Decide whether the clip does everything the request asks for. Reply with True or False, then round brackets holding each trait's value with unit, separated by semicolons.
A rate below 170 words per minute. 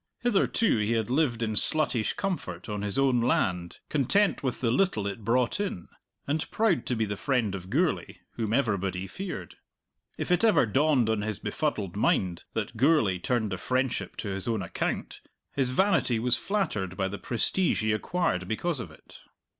False (180 wpm)